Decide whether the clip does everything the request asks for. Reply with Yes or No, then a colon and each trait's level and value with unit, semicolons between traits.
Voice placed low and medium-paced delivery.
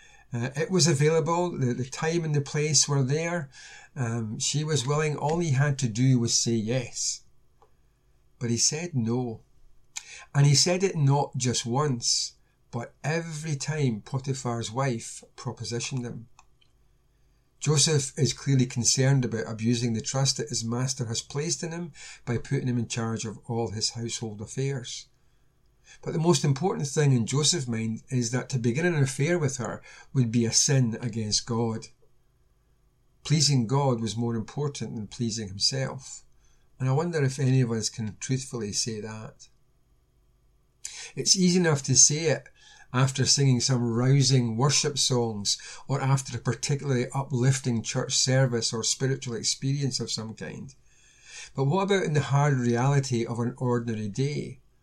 Yes: low, 130 Hz; average, 160 wpm